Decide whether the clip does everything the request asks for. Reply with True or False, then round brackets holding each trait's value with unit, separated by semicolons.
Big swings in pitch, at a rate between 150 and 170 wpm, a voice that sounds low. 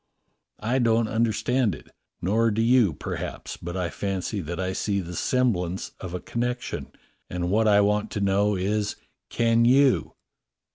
False (3.7 semitones; 165 wpm; 105 Hz)